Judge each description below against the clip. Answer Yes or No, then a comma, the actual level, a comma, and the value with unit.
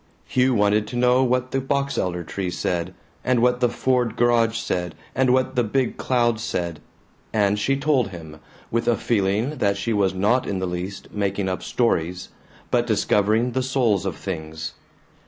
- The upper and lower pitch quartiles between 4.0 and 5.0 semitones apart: Yes, average, 4.7 semitones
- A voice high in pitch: No, low, 110 Hz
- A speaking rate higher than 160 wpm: Yes, average, 175 wpm